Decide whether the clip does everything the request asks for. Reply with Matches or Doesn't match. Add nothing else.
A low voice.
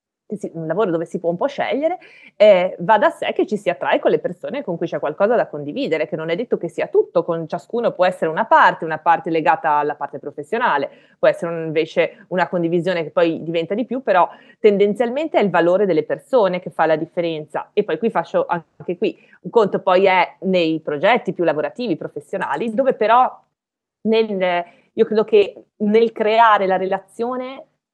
Doesn't match